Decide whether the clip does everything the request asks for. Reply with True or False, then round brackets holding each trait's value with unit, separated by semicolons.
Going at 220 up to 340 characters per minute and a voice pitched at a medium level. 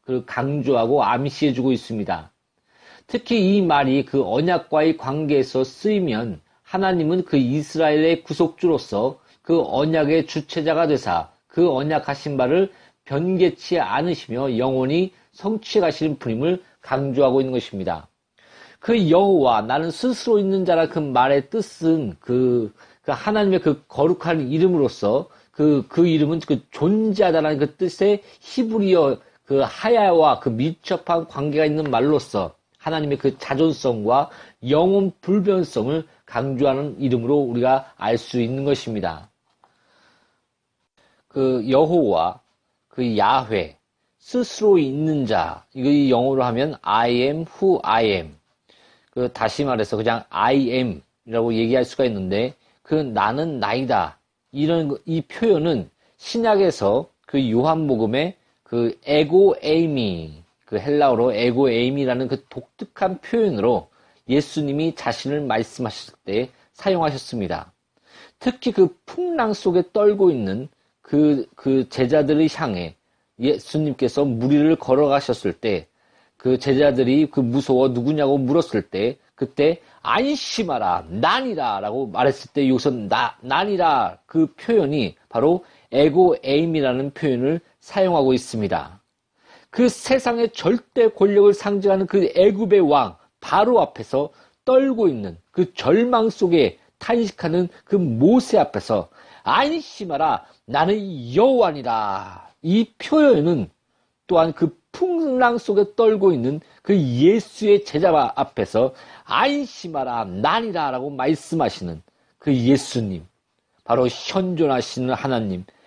True (265 characters per minute; 150 Hz)